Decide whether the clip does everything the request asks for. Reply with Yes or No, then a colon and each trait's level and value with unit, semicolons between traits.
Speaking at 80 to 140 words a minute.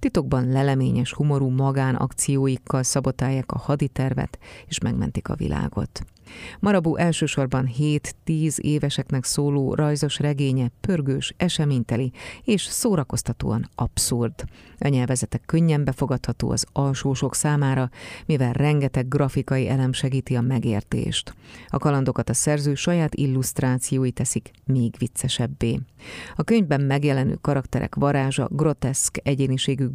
Yes: slow, 105 wpm